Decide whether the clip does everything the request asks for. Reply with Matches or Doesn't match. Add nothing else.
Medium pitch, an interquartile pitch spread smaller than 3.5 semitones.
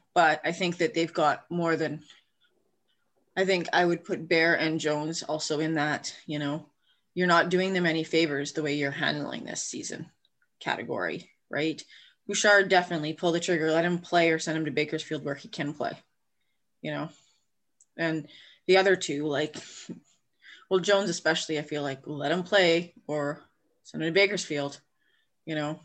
Matches